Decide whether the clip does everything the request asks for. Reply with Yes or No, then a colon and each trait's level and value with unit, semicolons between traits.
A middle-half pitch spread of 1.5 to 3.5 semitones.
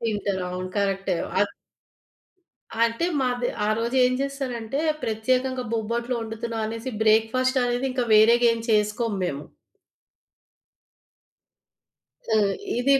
Yes: average, 2.7 semitones